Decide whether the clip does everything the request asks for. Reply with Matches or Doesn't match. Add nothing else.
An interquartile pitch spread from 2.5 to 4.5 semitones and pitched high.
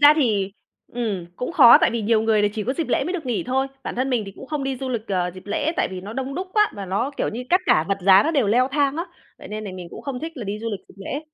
Doesn't match